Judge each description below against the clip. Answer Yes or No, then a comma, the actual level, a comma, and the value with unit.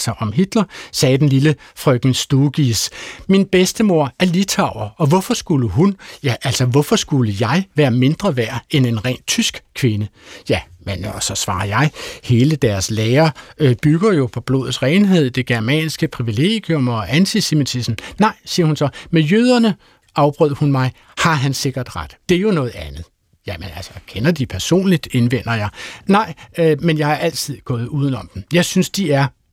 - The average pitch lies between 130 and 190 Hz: Yes, medium, 140 Hz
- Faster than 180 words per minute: No, average, 175 wpm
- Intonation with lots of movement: Yes, wide, 6.1 semitones